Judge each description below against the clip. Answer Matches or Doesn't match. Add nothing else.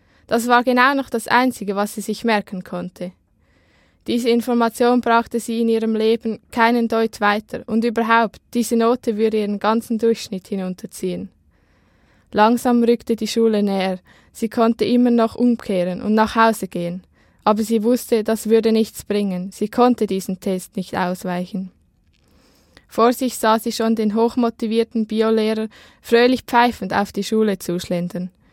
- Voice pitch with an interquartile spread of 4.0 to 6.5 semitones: Doesn't match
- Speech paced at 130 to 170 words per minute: Matches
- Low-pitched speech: Doesn't match